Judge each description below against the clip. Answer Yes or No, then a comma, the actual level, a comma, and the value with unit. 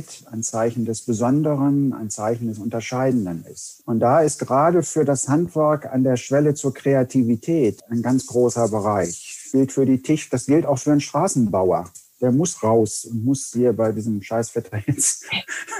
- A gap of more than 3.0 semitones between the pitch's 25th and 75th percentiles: Yes, average, 3.7 semitones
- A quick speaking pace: No, average, 175 wpm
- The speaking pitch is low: Yes, low, 130 Hz